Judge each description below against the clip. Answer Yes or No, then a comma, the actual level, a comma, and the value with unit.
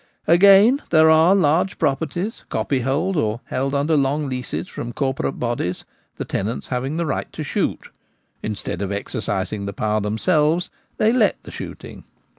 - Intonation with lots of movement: Yes, wide, 6.5 semitones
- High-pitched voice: No, medium, 140 Hz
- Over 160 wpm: No, average, 150 wpm